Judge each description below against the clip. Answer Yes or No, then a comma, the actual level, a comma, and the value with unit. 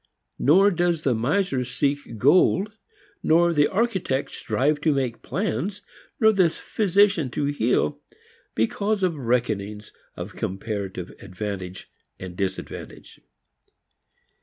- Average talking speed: No, slow, 110 wpm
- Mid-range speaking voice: Yes, medium, 145 Hz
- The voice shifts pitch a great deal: Yes, wide, 8.7 semitones